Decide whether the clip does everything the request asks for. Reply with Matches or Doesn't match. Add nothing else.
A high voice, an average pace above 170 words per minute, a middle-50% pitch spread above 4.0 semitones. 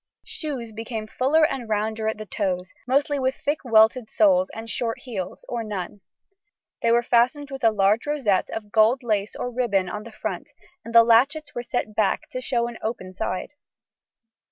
Doesn't match